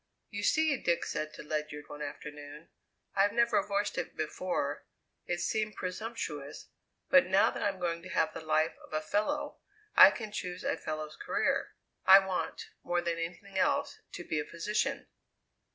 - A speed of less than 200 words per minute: Yes, average, 170 wpm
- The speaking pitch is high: No, medium, 180 Hz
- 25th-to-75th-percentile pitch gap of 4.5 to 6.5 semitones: Yes, average, 5.1 semitones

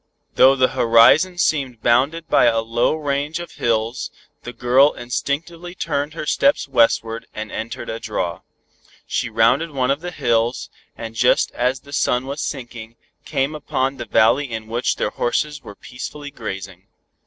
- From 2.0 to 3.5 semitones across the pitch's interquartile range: No, average, 4.1 semitones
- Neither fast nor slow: Yes, average, 160 wpm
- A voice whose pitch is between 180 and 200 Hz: No, low, 125 Hz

